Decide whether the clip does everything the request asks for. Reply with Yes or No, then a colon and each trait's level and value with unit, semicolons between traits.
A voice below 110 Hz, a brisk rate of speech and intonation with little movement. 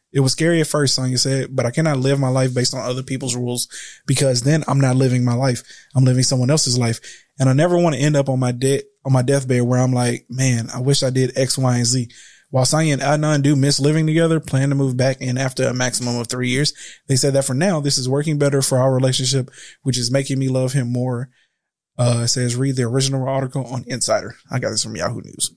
No: low, 130 Hz; fast, 255 wpm; narrow, 1.7 semitones